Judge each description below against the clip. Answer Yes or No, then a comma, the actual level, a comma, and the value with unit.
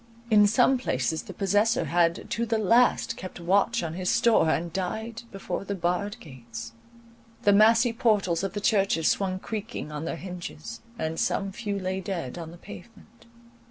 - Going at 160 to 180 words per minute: Yes, average, 170 wpm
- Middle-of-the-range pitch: No, high, 195 Hz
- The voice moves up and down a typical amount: Yes, average, 4.5 semitones